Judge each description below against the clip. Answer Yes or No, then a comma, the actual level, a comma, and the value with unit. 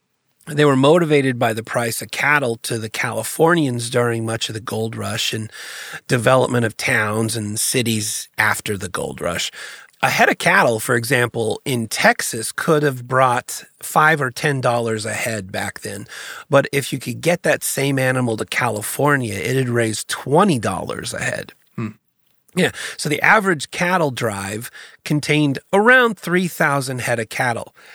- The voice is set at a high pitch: No, low, 125 Hz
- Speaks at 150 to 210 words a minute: Yes, average, 165 wpm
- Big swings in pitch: No, average, 4.5 semitones